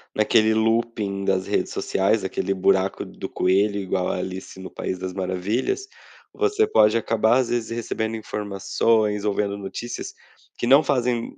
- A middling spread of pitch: Yes, average, 3.1 semitones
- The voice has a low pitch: Yes, low, 105 Hz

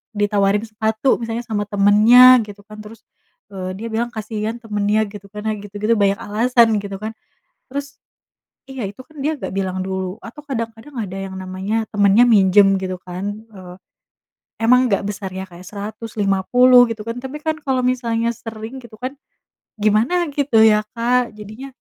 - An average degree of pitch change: Yes, average, 3.0 semitones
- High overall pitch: Yes, high, 215 Hz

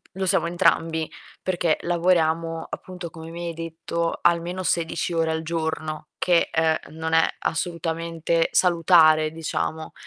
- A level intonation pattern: Yes, narrow, 1.1 semitones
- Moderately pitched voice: Yes, medium, 165 Hz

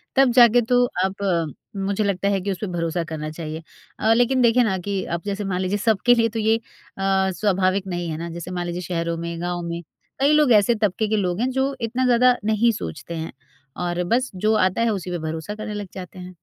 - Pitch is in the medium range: No, high, 195 Hz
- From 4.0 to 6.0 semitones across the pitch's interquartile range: Yes, average, 4.5 semitones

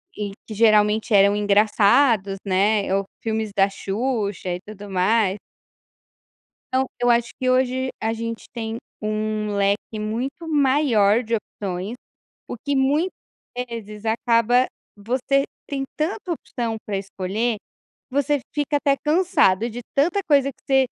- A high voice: Yes, high, 225 Hz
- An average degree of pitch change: Yes, average, 4.3 semitones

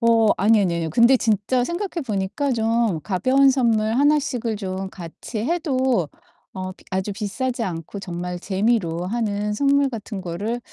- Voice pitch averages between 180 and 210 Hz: No, high, 220 Hz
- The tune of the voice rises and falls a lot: No, average, 5.0 semitones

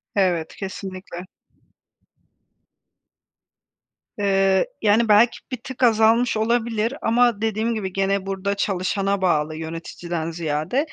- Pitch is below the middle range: No, high, 200 Hz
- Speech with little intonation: No, average, 3.4 semitones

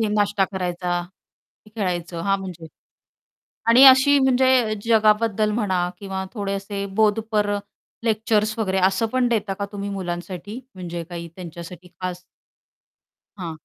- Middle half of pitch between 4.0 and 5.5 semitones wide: No, average, 3.3 semitones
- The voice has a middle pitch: No, high, 200 Hz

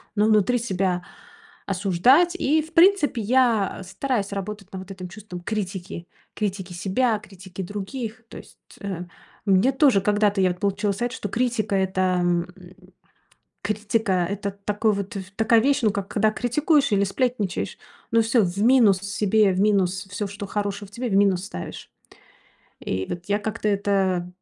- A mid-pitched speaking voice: No, high, 205 Hz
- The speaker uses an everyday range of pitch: Yes, average, 3.0 semitones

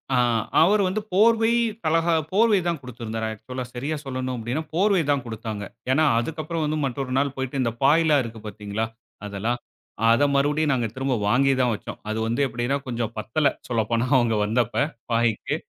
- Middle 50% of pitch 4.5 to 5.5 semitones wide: Yes, average, 5.1 semitones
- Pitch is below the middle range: Yes, low, 130 Hz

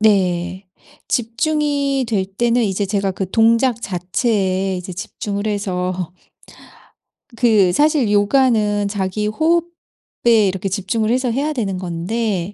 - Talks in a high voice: Yes, high, 205 Hz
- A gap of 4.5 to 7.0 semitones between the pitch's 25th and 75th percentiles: No, average, 4.0 semitones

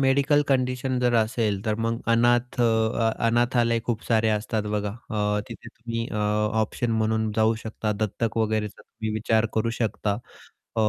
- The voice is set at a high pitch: No, low, 115 Hz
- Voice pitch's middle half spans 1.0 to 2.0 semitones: Yes, narrow, 1.7 semitones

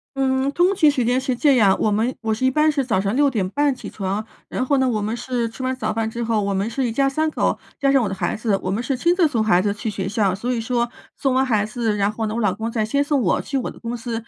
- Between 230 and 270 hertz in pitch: Yes, high, 235 Hz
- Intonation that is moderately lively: Yes, average, 3.7 semitones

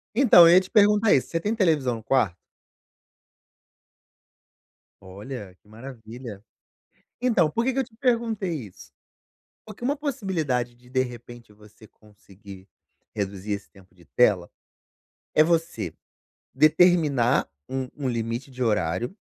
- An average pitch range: No, wide, 8.9 semitones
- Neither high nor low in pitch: No, low, 130 Hz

